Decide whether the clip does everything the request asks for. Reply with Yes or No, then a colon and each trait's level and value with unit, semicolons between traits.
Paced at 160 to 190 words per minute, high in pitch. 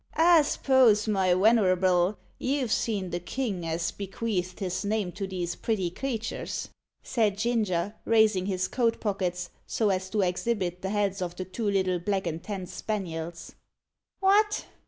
No: average, 150 wpm; high, 195 Hz